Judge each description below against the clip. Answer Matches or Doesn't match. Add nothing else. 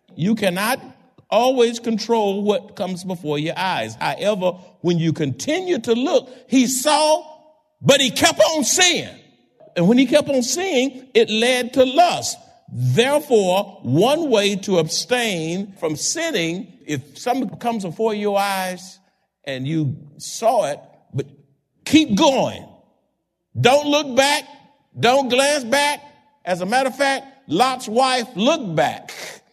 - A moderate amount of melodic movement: Doesn't match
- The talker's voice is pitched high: Matches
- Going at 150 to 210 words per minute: Doesn't match